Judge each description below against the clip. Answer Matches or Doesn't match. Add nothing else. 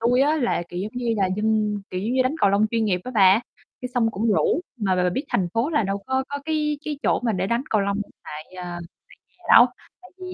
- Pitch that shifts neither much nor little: Matches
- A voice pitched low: Doesn't match